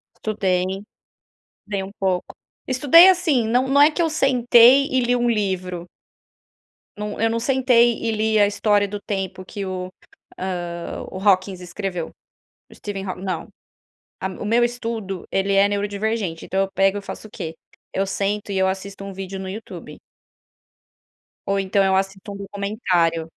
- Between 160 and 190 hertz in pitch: No, high, 200 Hz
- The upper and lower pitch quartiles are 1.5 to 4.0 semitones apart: Yes, average, 3.2 semitones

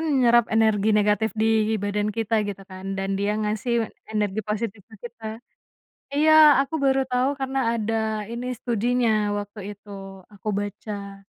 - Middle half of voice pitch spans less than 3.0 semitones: Yes, narrow, 2.5 semitones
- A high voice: Yes, high, 220 Hz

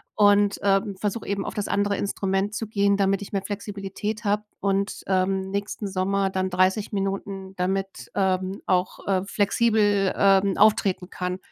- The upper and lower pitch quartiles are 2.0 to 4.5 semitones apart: No, narrow, 1.0 semitones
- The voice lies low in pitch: No, high, 195 Hz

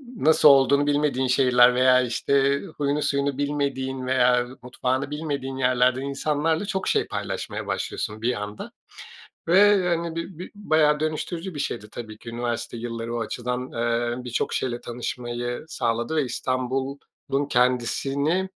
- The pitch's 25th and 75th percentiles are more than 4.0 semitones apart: No, average, 3.3 semitones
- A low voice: Yes, low, 130 Hz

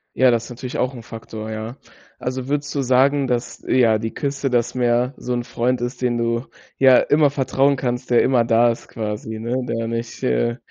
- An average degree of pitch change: No, narrow, 1.9 semitones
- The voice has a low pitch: Yes, low, 120 Hz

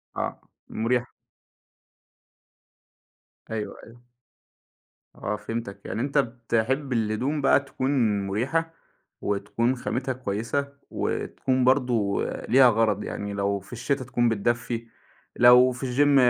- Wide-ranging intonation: No, average, 3.2 semitones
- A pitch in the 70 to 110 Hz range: No, low, 120 Hz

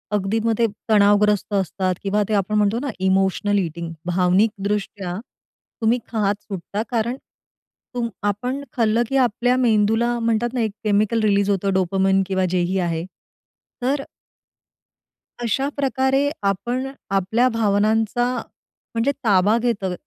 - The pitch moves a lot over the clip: No, average, 3.2 semitones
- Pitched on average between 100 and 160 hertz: No, high, 210 Hz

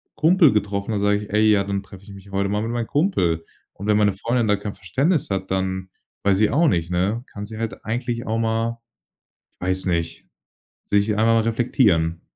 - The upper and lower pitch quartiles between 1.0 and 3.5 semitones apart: Yes, average, 2.9 semitones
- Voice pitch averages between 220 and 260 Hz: No, low, 105 Hz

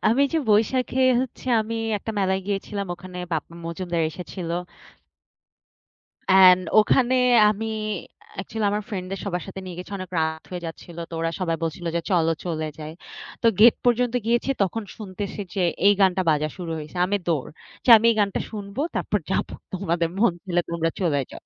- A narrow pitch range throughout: No, average, 3.7 semitones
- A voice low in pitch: No, high, 190 Hz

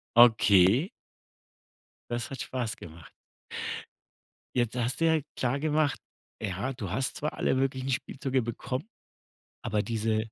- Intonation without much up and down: No, average, 3.5 semitones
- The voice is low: Yes, low, 125 Hz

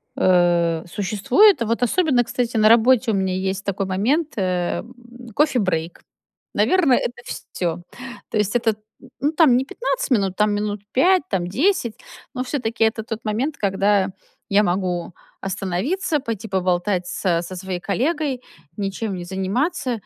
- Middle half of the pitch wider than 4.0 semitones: Yes, average, 5.3 semitones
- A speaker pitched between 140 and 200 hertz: No, high, 210 Hz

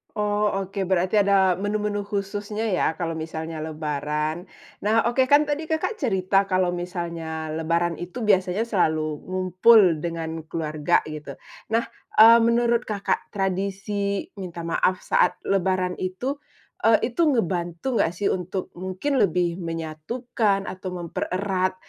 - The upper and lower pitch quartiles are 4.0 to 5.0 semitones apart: No, average, 3.3 semitones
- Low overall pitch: No, medium, 185 Hz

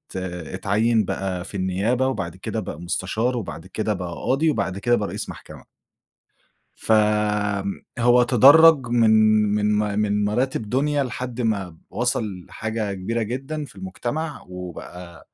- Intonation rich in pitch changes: No, average, 4.6 semitones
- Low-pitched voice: Yes, low, 110 Hz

